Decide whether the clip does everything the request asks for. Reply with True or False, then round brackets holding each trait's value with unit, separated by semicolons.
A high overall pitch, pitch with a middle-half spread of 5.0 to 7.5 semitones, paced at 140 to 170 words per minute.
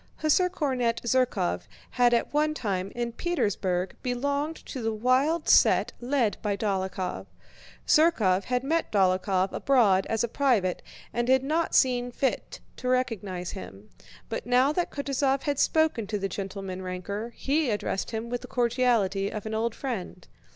True (235 Hz; 5.4 semitones; 155 wpm)